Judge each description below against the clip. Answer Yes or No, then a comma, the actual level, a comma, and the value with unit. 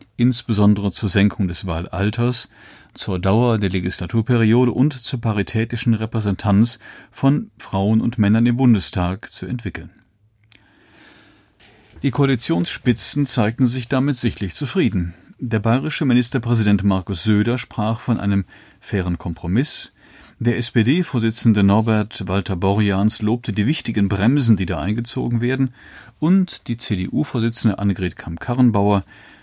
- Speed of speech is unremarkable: No, slow, 110 wpm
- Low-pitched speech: Yes, low, 110 Hz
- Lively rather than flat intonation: No, average, 3.5 semitones